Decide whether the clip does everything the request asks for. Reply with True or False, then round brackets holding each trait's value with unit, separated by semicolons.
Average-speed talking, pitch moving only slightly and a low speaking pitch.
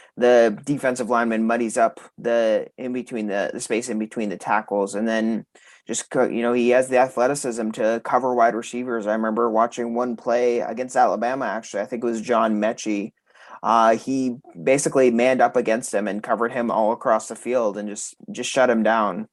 True (190 wpm; 2.0 semitones; 120 Hz)